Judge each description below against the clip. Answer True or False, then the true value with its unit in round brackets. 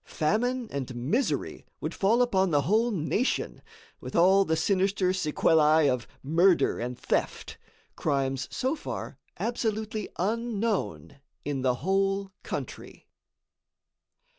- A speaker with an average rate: False (115 wpm)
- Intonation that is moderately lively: False (6.7 semitones)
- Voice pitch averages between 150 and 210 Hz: True (190 Hz)